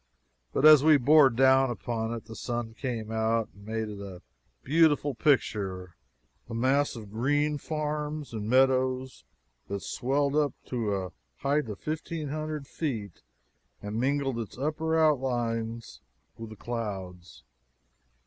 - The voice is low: Yes, low, 125 Hz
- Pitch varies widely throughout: No, average, 4.6 semitones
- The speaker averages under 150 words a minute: Yes, average, 140 wpm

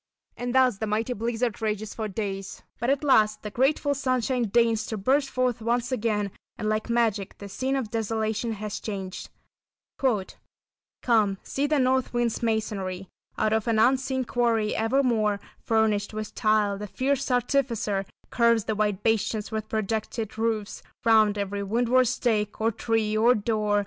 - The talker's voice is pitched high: Yes, high, 220 Hz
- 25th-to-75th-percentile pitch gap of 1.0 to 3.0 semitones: Yes, narrow, 2.5 semitones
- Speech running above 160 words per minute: No, average, 155 wpm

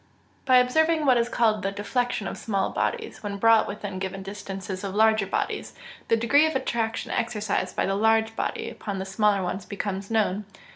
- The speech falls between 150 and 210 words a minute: Yes, average, 190 wpm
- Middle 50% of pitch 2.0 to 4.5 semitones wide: Yes, average, 3.0 semitones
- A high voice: Yes, high, 210 Hz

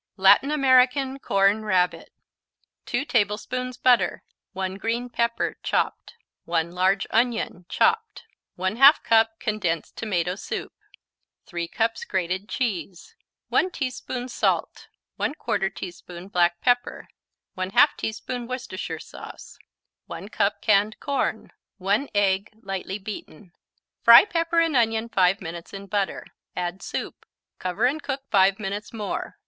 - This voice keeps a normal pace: No, slow, 120 wpm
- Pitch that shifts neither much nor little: Yes, average, 4.9 semitones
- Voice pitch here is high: Yes, high, 210 Hz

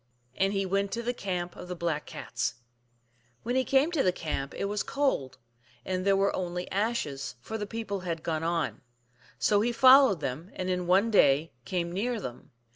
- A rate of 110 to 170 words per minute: No, average, 195 wpm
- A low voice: No, high, 190 Hz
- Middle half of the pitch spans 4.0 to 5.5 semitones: Yes, average, 4.6 semitones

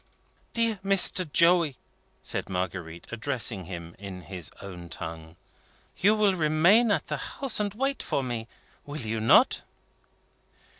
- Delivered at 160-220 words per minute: No, slow, 135 wpm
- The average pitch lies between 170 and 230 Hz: No, low, 130 Hz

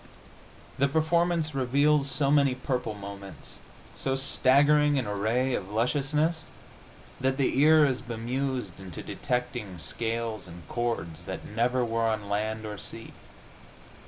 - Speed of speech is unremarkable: No, slow, 130 wpm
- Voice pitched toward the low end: Yes, low, 125 Hz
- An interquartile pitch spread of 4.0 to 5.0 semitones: Yes, average, 4.4 semitones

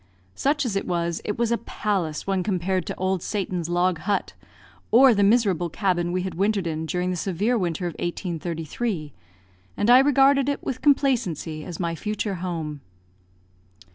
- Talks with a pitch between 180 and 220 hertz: Yes, medium, 185 Hz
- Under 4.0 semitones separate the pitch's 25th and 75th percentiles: No, average, 4.4 semitones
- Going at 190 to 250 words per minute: No, average, 170 wpm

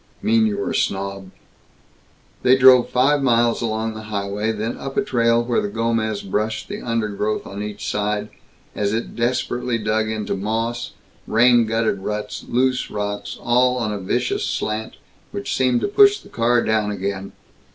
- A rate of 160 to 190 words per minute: Yes, average, 170 wpm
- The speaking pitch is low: Yes, low, 110 Hz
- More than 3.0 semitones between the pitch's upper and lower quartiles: No, narrow, 2.5 semitones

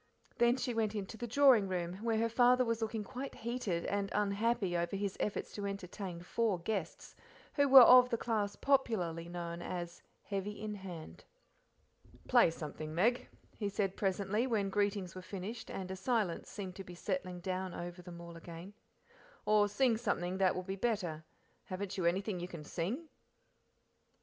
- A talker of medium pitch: No, high, 200 Hz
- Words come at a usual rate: Yes, average, 165 wpm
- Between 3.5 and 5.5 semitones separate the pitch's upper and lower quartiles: Yes, average, 4.1 semitones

